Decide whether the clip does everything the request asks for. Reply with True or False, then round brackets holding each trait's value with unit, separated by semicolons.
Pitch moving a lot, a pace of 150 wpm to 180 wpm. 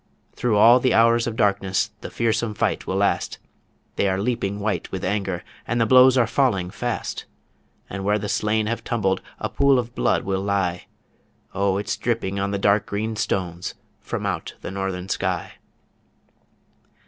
False (3.2 semitones; 170 wpm)